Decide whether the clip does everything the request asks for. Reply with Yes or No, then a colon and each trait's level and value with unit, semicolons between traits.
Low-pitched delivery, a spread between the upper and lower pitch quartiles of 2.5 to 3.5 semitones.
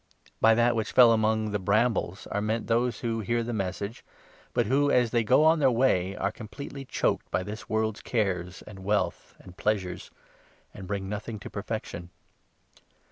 Yes: low, 110 Hz; average, 2.9 semitones